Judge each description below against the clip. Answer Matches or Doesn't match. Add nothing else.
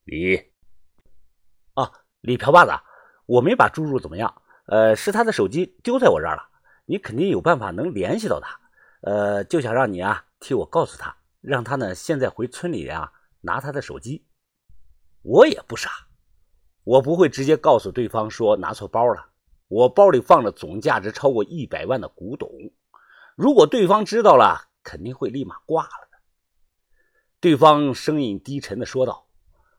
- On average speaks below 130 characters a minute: Doesn't match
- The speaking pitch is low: Matches